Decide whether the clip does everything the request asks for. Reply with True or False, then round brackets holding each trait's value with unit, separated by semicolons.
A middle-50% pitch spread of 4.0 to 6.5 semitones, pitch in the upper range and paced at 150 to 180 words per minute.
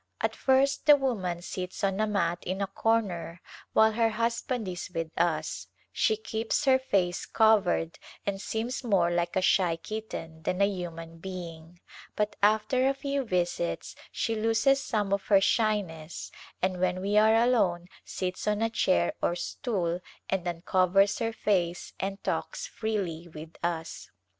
True (4.3 semitones; 195 Hz; 155 wpm)